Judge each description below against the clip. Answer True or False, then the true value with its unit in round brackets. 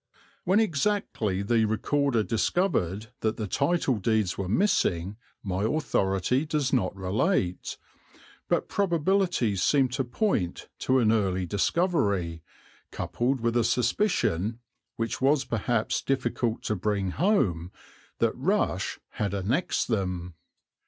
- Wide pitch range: True (6.5 semitones)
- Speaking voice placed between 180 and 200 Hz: False (115 Hz)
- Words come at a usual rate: False (120 wpm)